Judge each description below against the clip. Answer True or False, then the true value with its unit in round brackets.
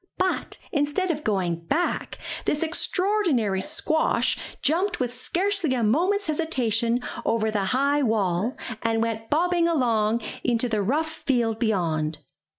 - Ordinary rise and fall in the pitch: False (6.6 semitones)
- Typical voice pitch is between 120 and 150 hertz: False (250 Hz)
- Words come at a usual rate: False (130 wpm)